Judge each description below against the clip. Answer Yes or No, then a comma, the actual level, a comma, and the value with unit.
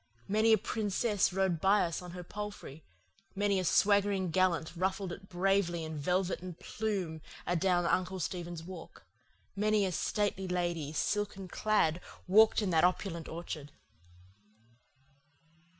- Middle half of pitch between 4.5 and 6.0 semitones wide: No, average, 2.8 semitones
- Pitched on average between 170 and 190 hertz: Yes, medium, 185 Hz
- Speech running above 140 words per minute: No, slow, 135 wpm